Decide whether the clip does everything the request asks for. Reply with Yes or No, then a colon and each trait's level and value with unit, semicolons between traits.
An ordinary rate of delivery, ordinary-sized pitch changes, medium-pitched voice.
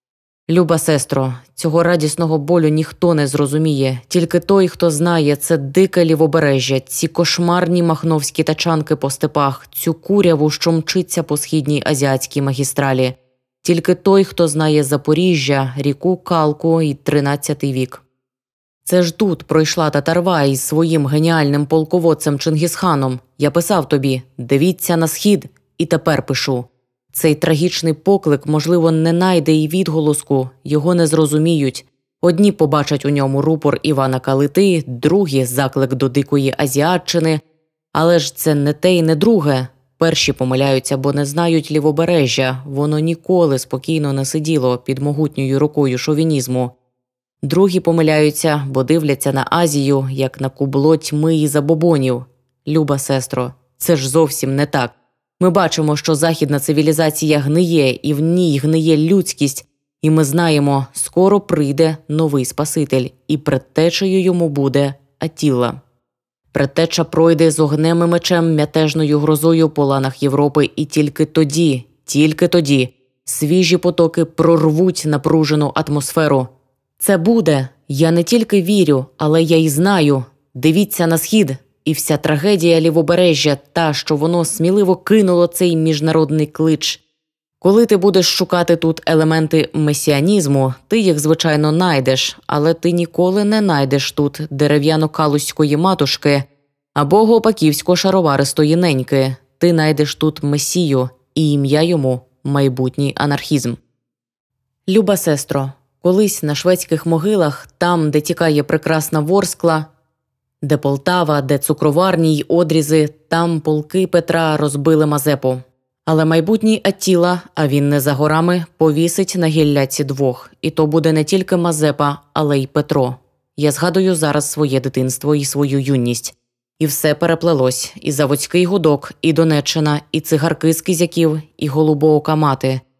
Yes: average, 130 wpm; average, 3.0 semitones; medium, 155 Hz